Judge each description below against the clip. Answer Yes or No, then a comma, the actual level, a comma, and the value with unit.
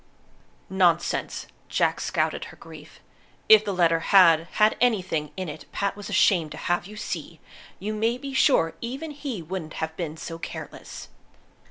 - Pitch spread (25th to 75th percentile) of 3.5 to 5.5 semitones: Yes, average, 4.7 semitones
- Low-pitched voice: No, high, 190 Hz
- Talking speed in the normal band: Yes, average, 160 wpm